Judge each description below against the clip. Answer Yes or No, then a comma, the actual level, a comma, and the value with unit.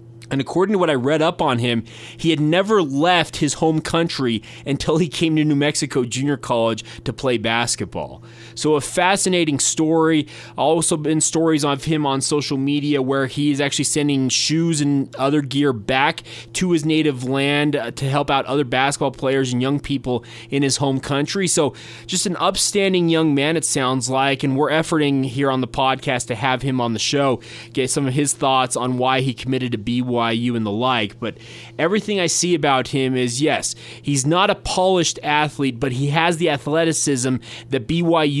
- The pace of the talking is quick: No, average, 190 wpm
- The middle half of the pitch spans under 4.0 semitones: Yes, average, 3.6 semitones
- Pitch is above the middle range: No, medium, 140 Hz